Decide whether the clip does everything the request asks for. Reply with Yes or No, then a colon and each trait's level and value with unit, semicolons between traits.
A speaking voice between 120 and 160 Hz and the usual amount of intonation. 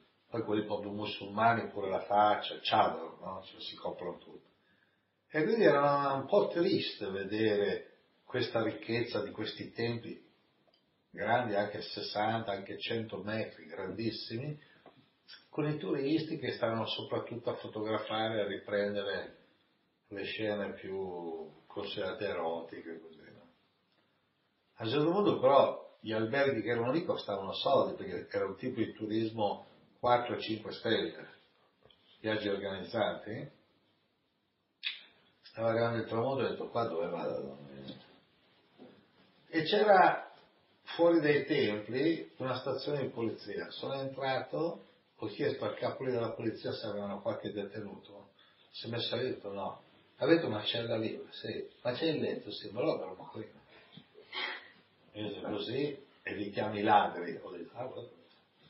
No: low, 110 Hz; average, 3.2 semitones